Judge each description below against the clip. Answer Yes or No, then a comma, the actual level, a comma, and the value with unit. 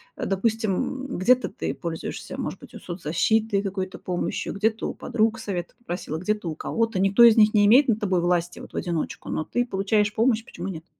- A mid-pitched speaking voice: No, high, 205 Hz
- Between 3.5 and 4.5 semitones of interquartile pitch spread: Yes, average, 4.0 semitones